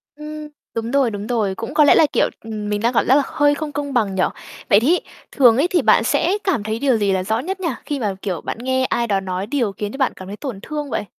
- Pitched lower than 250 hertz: Yes, high, 240 Hz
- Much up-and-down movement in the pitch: Yes, wide, 5.8 semitones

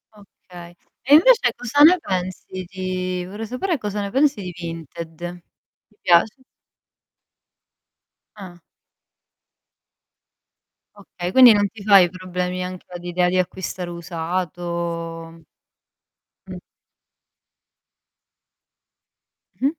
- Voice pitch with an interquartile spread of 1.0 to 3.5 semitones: Yes, average, 2.9 semitones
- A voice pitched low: No, medium, 185 Hz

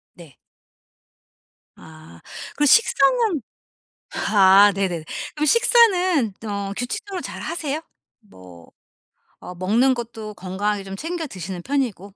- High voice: Yes, high, 210 Hz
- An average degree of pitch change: No, wide, 8.4 semitones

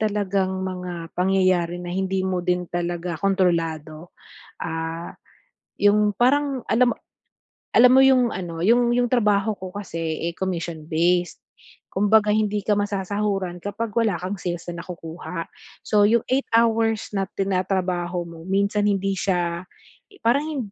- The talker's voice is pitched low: No, high, 190 Hz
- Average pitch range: Yes, average, 3.2 semitones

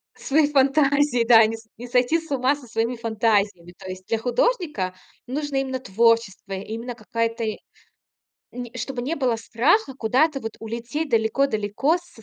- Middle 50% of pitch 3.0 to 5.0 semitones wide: Yes, average, 3.6 semitones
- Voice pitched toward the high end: Yes, high, 240 Hz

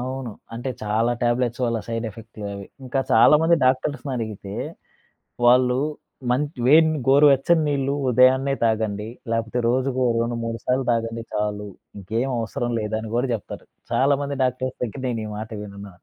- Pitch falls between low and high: No, low, 120 Hz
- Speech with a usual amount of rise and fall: Yes, average, 3.1 semitones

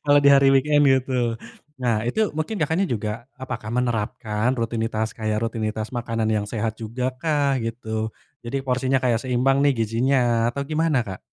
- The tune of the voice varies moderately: Yes, average, 3.4 semitones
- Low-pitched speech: Yes, low, 120 Hz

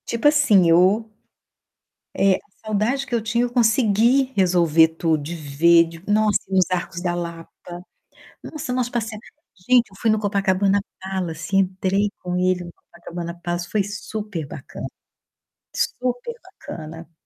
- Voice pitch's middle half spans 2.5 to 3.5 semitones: No, average, 4.6 semitones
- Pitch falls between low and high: No, high, 195 Hz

